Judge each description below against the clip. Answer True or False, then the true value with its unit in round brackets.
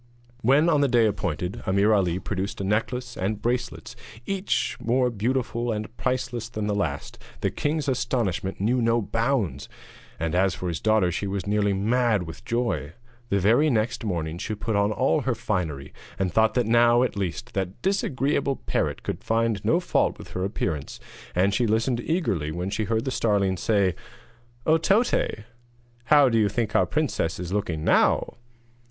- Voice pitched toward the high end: False (110 Hz)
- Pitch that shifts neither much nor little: True (4.4 semitones)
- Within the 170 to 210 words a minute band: True (175 wpm)